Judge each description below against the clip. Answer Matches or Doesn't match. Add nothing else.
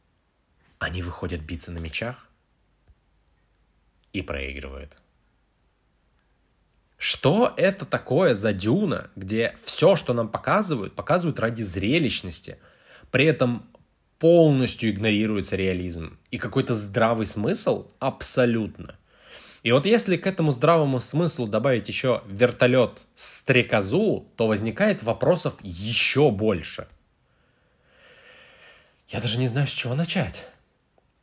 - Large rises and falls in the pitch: Matches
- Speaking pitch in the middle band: Doesn't match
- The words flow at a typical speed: Doesn't match